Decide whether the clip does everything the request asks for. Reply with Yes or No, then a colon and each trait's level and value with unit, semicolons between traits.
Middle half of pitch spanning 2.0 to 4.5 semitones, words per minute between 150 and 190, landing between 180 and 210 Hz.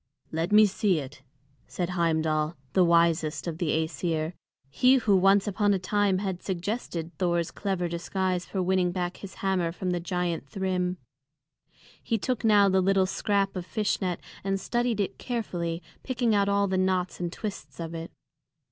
Yes: average, 2.8 semitones; average, 170 wpm; medium, 185 Hz